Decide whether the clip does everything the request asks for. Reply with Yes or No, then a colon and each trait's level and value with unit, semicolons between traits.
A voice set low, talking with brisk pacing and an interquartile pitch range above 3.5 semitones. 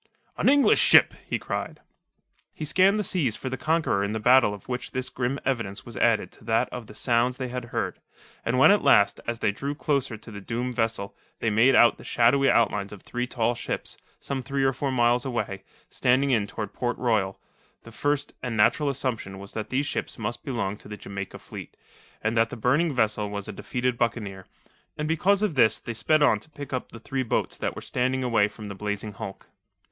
Yes: low, 120 Hz; fast, 215 wpm; average, 3.9 semitones